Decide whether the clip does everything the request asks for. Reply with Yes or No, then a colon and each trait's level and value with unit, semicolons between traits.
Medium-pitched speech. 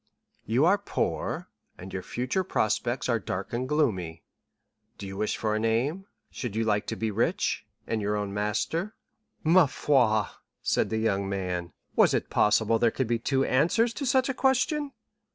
No: low, 115 Hz